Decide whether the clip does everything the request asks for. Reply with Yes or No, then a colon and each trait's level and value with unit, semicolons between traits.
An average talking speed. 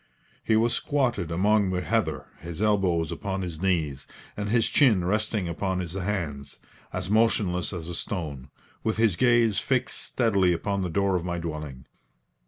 Yes: average, 165 wpm